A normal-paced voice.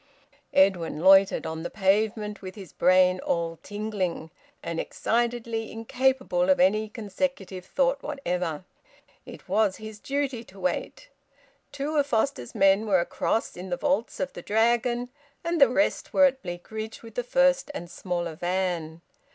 Yes: average, 145 wpm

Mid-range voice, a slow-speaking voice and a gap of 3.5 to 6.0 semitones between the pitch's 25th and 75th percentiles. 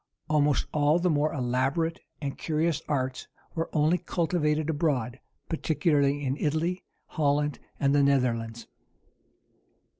No: medium, 150 Hz; slow, 115 wpm; narrow, 2.5 semitones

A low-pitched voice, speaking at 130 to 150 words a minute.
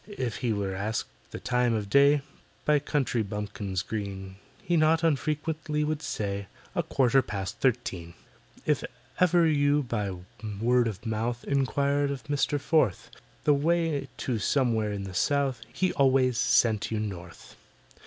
Yes: low, 125 Hz; average, 145 wpm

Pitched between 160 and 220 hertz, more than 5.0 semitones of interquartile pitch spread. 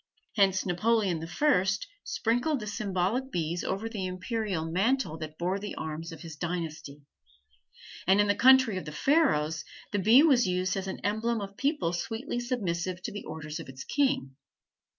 Yes: high, 190 Hz; wide, 5.4 semitones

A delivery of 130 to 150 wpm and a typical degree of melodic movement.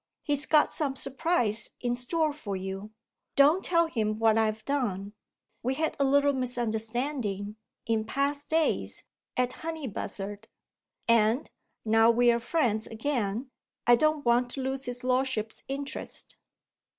Yes: slow, 135 wpm; average, 4.5 semitones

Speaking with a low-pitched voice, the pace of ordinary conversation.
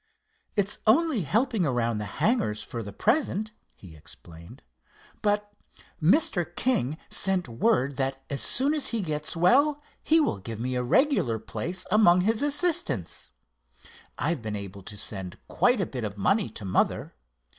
No: medium, 170 Hz; average, 155 wpm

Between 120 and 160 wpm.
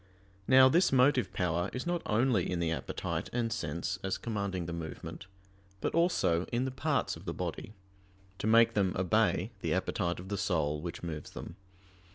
No: average, 180 wpm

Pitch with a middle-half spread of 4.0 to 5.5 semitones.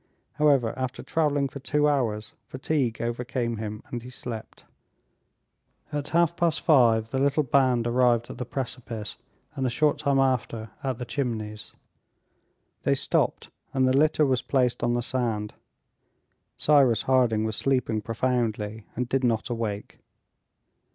No: average, 3.2 semitones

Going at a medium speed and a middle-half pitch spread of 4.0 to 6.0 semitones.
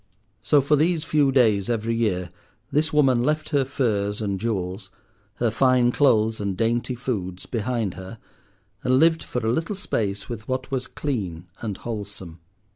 Yes: average, 160 wpm; average, 4.9 semitones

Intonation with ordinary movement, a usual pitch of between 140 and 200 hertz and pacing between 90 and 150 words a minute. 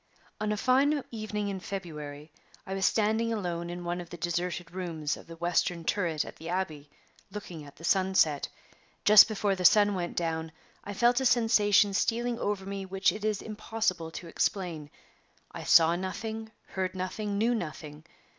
No: average, 3.9 semitones; high, 190 Hz; average, 175 wpm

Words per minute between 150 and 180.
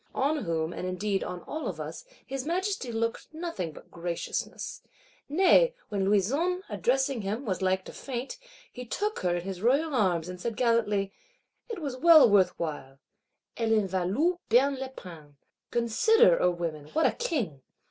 Yes: average, 170 wpm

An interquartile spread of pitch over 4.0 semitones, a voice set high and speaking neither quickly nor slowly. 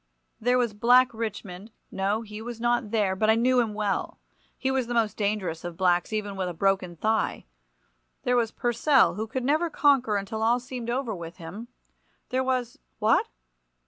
No: average, 3.5 semitones; high, 225 Hz; average, 175 wpm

